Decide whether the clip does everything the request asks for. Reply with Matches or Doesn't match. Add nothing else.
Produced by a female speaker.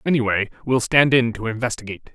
Doesn't match